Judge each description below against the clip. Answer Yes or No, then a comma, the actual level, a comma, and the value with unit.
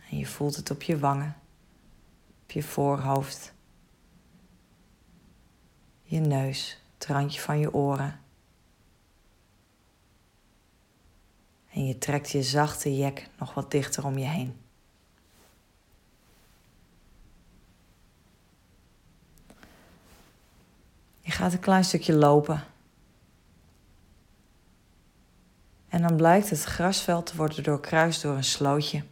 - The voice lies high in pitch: No, medium, 140 Hz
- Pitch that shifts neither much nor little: No, wide, 7.0 semitones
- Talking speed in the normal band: No, slow, 95 wpm